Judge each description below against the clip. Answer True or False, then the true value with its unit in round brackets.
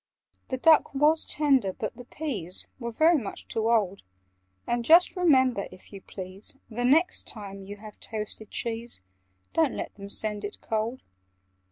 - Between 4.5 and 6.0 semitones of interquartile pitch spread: True (5.1 semitones)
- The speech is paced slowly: False (160 wpm)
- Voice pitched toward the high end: True (230 Hz)